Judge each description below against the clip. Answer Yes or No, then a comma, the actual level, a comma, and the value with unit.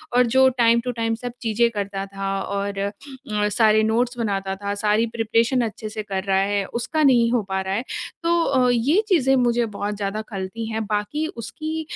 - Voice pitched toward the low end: No, high, 225 Hz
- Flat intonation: No, average, 3.3 semitones